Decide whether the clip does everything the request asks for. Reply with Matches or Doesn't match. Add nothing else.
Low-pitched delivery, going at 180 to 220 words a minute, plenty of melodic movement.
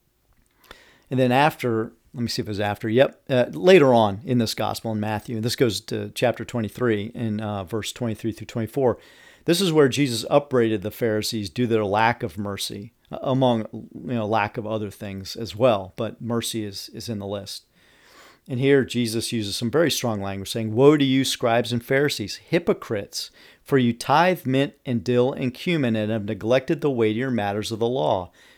Doesn't match